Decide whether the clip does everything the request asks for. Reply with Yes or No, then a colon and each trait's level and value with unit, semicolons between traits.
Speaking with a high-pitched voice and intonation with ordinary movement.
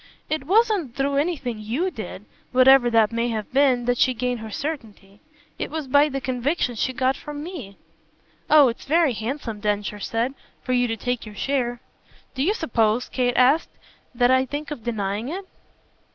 Yes: very high, 255 Hz; average, 3.9 semitones